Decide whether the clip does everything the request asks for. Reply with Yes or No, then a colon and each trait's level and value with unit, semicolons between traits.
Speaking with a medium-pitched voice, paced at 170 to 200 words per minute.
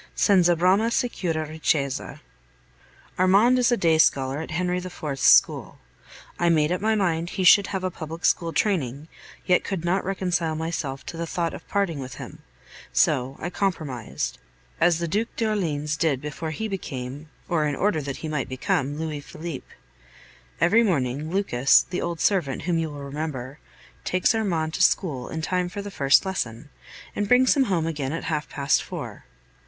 Yes: medium, 165 Hz; average, 175 wpm